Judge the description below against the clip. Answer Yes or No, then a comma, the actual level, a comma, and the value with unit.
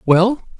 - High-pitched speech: Yes, high, 210 Hz